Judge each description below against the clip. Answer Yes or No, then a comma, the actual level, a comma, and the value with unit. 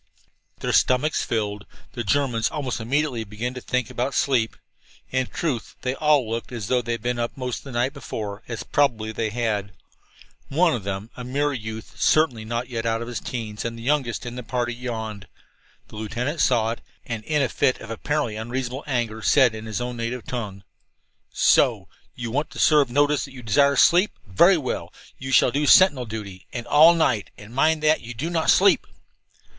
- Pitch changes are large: No, average, 3.7 semitones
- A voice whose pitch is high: No, low, 120 Hz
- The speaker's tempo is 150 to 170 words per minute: No, average, 195 wpm